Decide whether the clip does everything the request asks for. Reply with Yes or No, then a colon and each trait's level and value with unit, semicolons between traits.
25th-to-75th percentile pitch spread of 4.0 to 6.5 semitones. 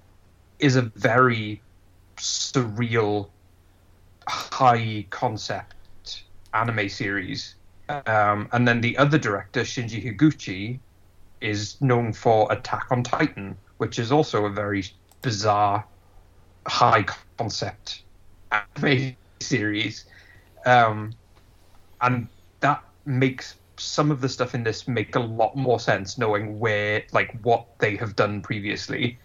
Yes: average, 4.4 semitones